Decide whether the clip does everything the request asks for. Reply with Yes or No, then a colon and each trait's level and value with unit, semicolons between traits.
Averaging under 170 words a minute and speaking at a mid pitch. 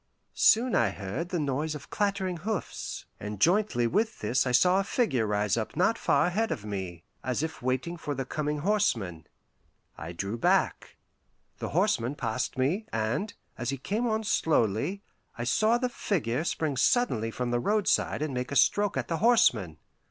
No: average, 175 wpm; medium, 145 Hz